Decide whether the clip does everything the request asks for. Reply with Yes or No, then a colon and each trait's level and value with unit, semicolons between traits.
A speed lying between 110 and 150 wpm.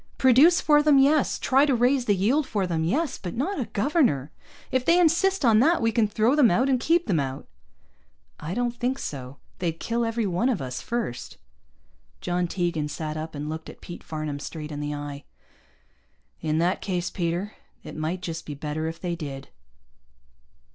No: average, 190 wpm